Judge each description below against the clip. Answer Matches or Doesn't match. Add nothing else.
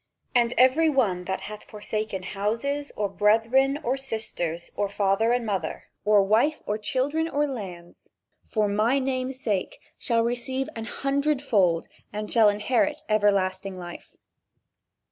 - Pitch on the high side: Matches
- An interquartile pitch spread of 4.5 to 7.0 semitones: Matches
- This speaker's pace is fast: Doesn't match